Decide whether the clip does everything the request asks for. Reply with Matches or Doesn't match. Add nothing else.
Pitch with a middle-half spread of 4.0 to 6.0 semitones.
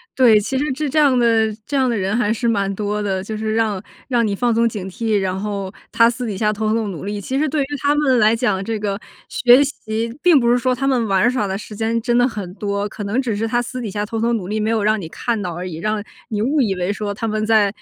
Doesn't match